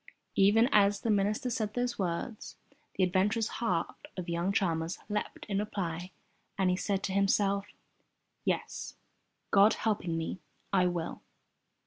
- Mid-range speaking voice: No, high, 195 Hz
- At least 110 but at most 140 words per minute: Yes, slow, 135 wpm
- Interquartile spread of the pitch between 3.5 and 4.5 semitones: No, narrow, 2.6 semitones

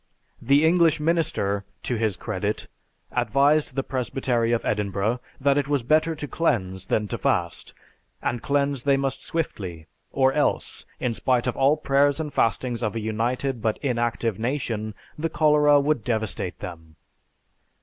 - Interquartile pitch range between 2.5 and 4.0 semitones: No, average, 4.7 semitones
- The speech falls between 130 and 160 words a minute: Yes, average, 150 wpm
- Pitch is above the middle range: No, low, 125 Hz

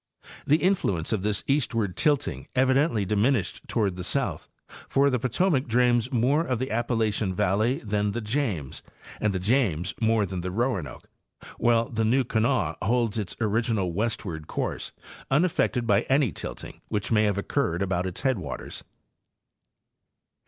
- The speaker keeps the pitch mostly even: No, average, 4.6 semitones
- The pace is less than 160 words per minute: Yes, average, 150 wpm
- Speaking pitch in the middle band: No, low, 110 Hz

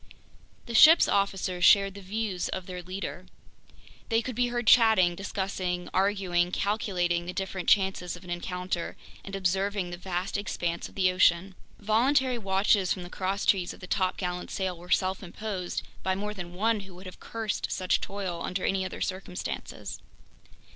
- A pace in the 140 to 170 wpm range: Yes, average, 165 wpm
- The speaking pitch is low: No, high, 190 Hz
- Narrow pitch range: Yes, narrow, 2.0 semitones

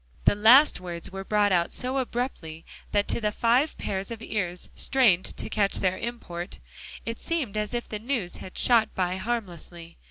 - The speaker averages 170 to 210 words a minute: Yes, average, 180 wpm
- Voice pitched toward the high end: Yes, high, 210 Hz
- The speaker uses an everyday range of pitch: Yes, average, 4.7 semitones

